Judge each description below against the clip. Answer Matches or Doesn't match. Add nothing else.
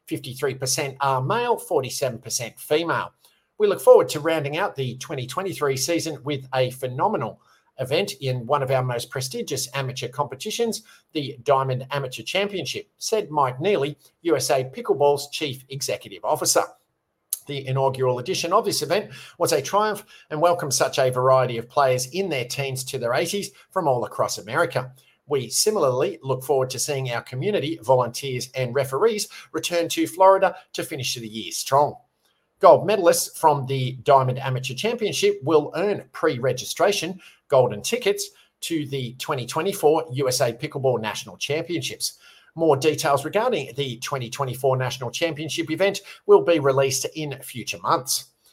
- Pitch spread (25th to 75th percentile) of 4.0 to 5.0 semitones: Matches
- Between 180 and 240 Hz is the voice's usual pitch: Doesn't match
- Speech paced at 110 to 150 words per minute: Matches